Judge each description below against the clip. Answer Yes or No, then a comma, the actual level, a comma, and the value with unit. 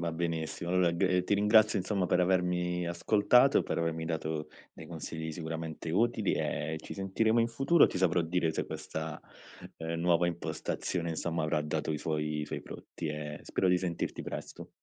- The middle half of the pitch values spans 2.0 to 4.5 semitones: Yes, narrow, 2.4 semitones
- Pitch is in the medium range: No, very low, 85 Hz